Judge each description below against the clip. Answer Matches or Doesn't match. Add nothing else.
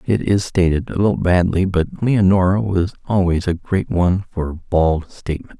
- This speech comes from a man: Matches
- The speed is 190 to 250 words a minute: Doesn't match